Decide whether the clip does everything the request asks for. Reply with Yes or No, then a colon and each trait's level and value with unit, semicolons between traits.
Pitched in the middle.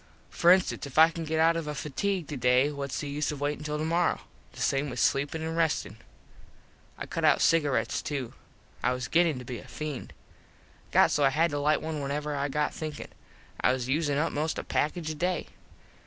Yes: medium, 150 Hz